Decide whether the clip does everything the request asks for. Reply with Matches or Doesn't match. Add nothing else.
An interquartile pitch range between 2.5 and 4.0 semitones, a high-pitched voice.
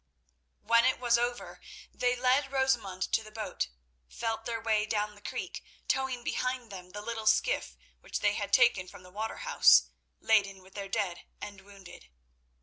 Matches